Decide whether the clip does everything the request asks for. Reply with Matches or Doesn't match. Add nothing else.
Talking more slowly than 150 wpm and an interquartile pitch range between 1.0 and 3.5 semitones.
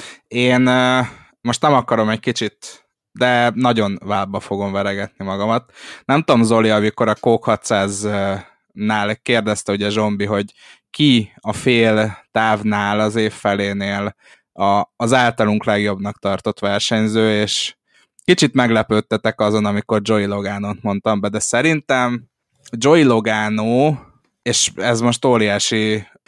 Matches